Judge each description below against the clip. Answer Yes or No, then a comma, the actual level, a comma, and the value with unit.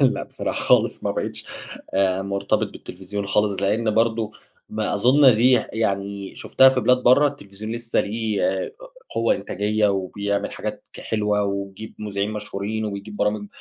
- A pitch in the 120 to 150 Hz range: No, low, 105 Hz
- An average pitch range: No, narrow, 2.1 semitones